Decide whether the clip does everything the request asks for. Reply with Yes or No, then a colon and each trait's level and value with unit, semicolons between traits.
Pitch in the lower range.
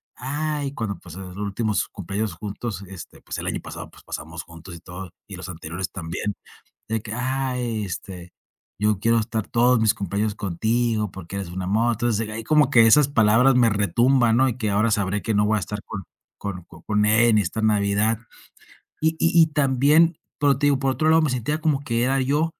Yes: low, 110 Hz